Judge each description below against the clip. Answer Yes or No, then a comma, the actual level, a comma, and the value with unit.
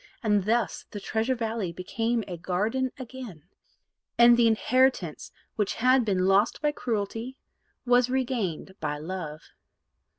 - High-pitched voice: Yes, high, 225 Hz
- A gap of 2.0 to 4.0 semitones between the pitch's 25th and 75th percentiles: No, average, 4.7 semitones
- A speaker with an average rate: No, slow, 130 wpm